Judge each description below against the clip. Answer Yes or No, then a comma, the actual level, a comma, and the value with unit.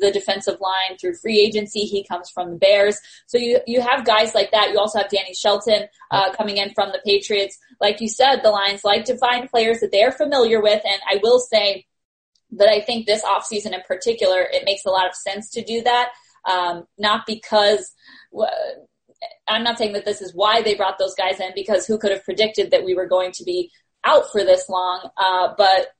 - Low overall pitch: No, high, 210 Hz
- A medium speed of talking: No, fast, 215 wpm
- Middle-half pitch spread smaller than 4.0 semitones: Yes, average, 2.8 semitones